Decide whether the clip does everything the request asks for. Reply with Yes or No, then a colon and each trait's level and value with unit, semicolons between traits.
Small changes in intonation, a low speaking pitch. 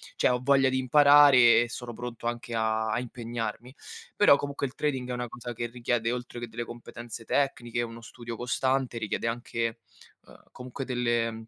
Yes: narrow, 1.5 semitones; low, 120 Hz